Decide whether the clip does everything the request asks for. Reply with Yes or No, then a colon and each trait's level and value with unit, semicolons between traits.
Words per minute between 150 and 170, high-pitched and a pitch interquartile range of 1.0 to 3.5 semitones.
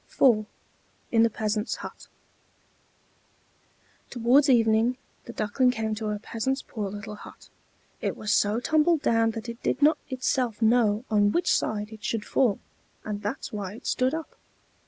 Yes: average, 155 wpm; high, 225 Hz; average, 3.1 semitones